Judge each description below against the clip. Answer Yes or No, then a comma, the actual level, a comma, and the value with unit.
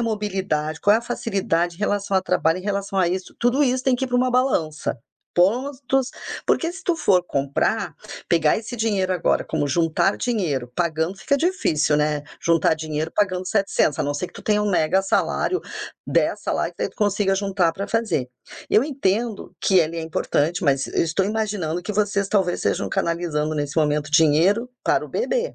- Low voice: No, high, 190 Hz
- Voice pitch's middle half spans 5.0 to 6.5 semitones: Yes, wide, 5.4 semitones